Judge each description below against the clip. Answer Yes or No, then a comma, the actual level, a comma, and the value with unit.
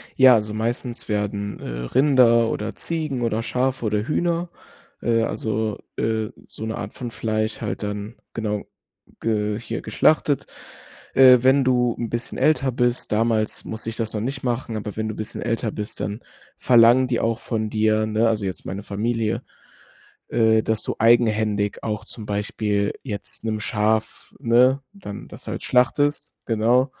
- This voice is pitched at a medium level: No, low, 115 Hz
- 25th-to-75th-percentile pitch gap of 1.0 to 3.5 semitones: Yes, narrow, 2.4 semitones